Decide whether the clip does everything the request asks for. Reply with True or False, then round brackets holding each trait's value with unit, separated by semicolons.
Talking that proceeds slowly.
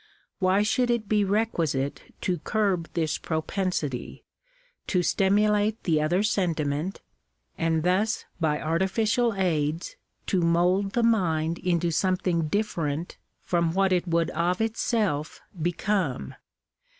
True (115 wpm)